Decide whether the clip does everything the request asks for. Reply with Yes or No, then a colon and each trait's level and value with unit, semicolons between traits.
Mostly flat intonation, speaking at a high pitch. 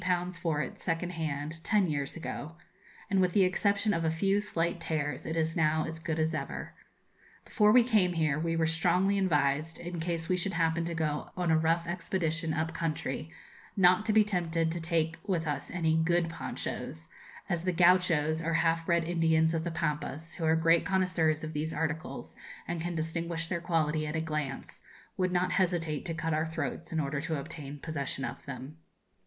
No: narrow, 1.8 semitones; medium, 165 Hz